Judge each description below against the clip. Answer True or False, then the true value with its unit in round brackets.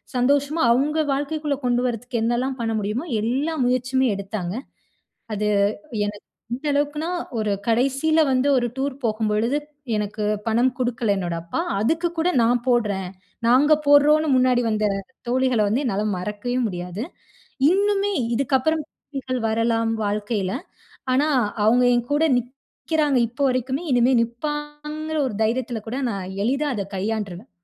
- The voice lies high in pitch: True (245 Hz)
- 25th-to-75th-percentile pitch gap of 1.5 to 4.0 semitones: False (4.7 semitones)